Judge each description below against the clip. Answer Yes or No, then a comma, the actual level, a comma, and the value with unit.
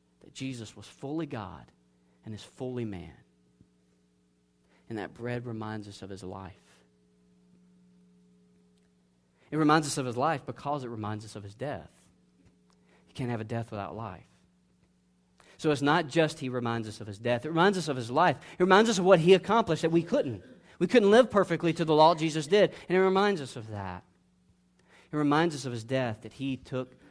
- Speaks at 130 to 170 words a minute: No, average, 195 wpm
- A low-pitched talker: Yes, low, 110 Hz